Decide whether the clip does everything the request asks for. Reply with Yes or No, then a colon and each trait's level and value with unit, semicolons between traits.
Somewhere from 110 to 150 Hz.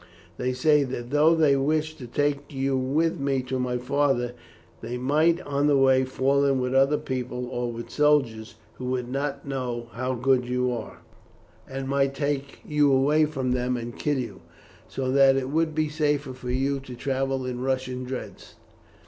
Yes: low, 135 Hz